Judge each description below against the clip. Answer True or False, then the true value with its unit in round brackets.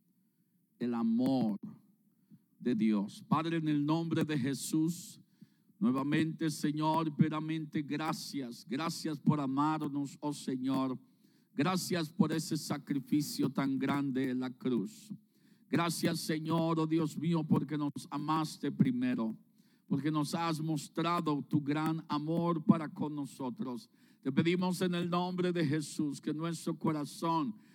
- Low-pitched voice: False (160 Hz)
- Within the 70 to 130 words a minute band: True (125 wpm)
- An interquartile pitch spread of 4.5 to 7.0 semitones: False (3.8 semitones)